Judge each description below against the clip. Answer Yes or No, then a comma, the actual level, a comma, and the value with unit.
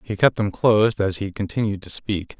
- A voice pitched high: No, low, 105 Hz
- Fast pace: Yes, fast, 225 wpm